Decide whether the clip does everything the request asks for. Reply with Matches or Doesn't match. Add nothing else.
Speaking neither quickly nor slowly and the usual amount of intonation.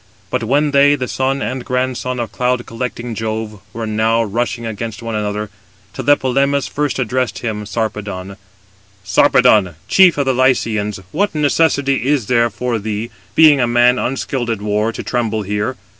Matches